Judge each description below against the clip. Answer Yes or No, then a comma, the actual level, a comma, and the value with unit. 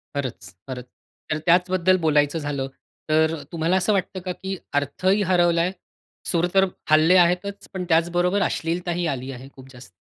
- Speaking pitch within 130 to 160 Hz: No, medium, 170 Hz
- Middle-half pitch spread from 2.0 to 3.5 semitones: No, average, 4.0 semitones